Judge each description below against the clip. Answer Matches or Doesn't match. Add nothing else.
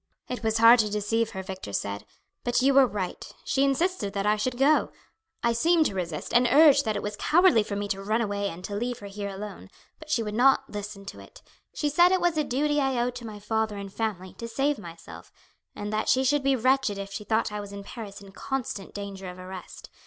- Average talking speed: Doesn't match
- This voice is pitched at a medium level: Doesn't match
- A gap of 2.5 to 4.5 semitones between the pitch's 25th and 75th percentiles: Doesn't match